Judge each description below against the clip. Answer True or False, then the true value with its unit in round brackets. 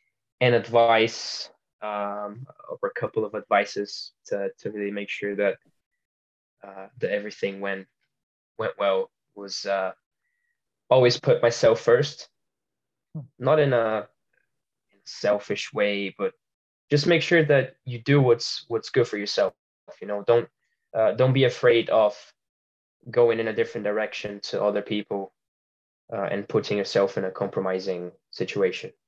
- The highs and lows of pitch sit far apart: True (5.9 semitones)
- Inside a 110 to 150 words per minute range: True (140 wpm)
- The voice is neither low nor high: False (110 Hz)